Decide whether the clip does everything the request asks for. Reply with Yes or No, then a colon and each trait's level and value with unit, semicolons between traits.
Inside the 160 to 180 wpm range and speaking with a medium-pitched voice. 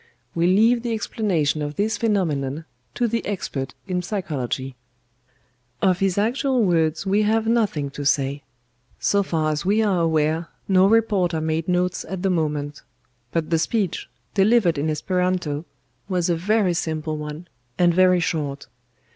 No: average, 150 wpm; medium, 175 Hz